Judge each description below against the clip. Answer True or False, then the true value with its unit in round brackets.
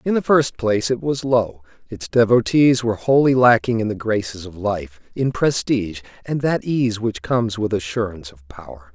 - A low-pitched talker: True (110 Hz)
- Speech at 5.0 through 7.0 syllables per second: True (5.1 syllables/s)